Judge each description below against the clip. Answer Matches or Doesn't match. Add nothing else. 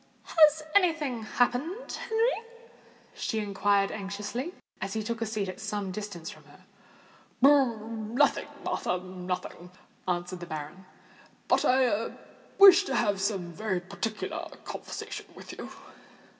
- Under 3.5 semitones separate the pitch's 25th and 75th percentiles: Doesn't match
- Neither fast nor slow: Doesn't match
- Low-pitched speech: Doesn't match